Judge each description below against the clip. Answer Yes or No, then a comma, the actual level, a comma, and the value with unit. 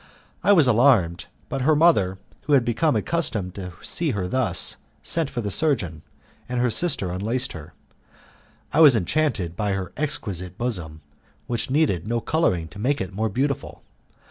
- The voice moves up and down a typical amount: No, wide, 7.5 semitones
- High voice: No, low, 115 Hz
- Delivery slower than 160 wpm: No, average, 165 wpm